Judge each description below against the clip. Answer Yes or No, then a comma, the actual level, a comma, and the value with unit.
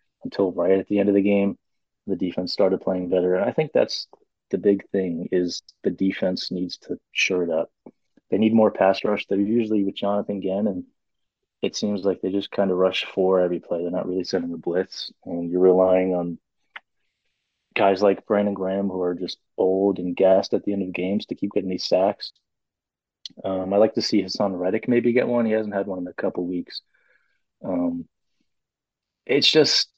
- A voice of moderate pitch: No, very low, 95 Hz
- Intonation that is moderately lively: No, narrow, 1.7 semitones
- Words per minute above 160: Yes, fast, 205 wpm